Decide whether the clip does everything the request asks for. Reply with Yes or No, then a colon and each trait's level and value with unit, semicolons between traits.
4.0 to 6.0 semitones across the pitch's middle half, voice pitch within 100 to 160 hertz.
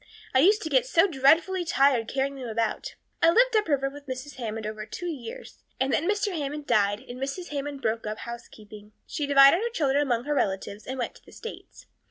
No: wide, 5.6 semitones; very high, 275 Hz